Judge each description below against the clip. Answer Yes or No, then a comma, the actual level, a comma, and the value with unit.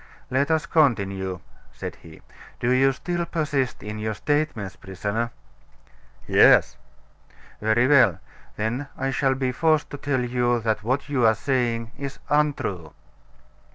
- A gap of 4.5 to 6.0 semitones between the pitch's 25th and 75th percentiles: Yes, average, 4.8 semitones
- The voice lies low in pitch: Yes, low, 125 Hz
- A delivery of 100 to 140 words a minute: Yes, slow, 135 wpm